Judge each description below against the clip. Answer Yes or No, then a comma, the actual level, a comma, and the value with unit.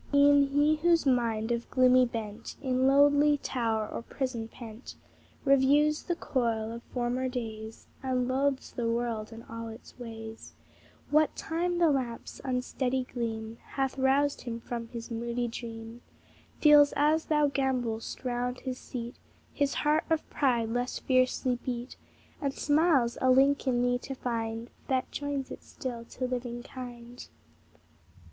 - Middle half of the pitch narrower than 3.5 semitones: Yes, average, 3.0 semitones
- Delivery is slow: No, average, 145 wpm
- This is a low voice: No, very high, 250 Hz